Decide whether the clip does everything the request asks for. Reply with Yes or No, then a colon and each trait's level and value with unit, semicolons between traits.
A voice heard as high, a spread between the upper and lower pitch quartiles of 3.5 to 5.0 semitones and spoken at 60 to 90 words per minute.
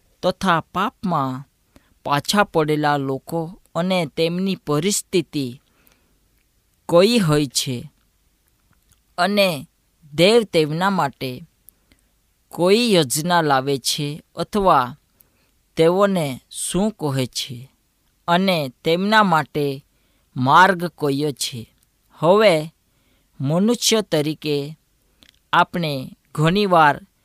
No: medium, 160 Hz; average, 4.4 semitones; average, 75 wpm